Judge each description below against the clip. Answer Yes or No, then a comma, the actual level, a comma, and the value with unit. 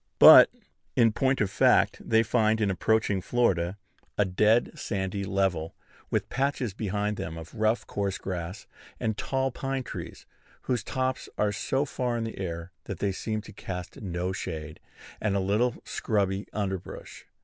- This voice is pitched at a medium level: No, low, 105 Hz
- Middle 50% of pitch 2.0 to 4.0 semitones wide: Yes, average, 3.4 semitones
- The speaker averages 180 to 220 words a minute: No, average, 160 wpm